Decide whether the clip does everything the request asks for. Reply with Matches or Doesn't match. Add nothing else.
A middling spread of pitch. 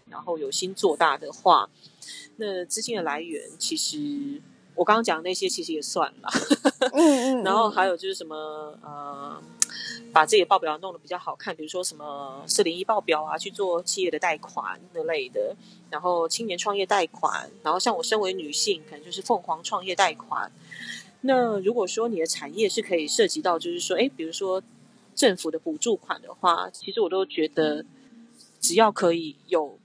Doesn't match